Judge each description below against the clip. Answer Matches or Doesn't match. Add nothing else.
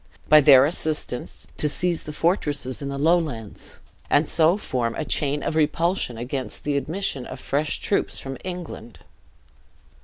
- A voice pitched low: Doesn't match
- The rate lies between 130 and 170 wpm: Matches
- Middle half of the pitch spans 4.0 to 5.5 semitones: Doesn't match